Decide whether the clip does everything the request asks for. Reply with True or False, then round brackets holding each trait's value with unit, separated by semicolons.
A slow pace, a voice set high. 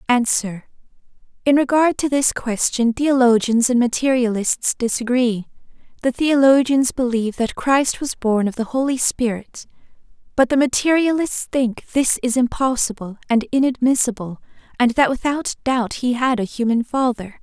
True (130 wpm; 250 Hz)